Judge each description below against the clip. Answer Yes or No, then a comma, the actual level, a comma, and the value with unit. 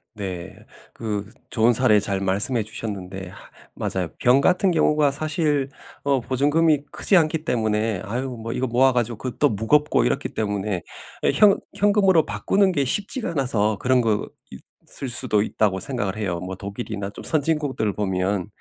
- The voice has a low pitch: Yes, low, 115 Hz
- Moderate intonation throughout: No, wide, 6.1 semitones